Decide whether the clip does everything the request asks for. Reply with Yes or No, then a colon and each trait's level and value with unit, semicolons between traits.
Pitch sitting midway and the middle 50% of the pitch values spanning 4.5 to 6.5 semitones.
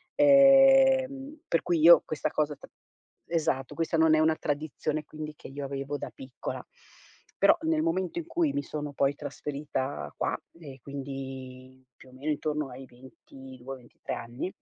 Yes: medium, 150 Hz; average, 4.8 semitones